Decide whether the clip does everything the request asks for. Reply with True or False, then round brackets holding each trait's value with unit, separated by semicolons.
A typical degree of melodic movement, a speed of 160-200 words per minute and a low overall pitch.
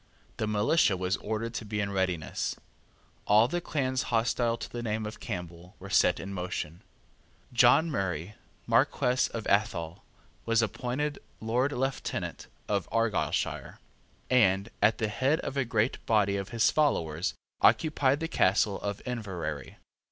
False (4.4 semitones; 145 wpm; 110 Hz)